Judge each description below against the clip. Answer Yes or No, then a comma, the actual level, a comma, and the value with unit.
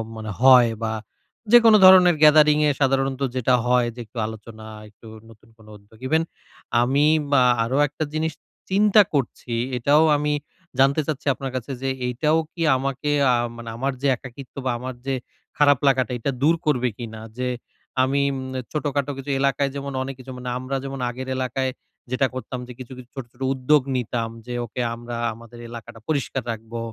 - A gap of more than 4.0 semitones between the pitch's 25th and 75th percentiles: No, average, 2.8 semitones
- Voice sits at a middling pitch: No, low, 130 Hz